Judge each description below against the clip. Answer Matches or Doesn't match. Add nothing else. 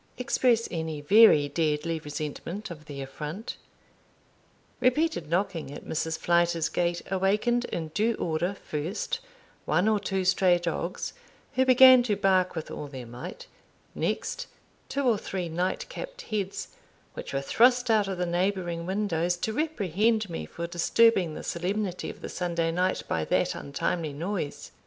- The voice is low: Doesn't match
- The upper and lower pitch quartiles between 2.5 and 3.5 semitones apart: Doesn't match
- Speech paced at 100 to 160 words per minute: Matches